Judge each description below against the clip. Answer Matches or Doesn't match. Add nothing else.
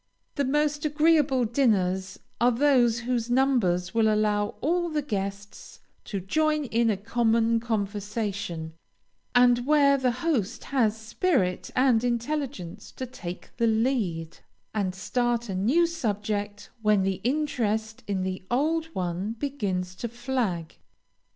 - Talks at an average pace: Doesn't match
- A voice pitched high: Matches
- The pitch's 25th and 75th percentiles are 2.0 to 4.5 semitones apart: Doesn't match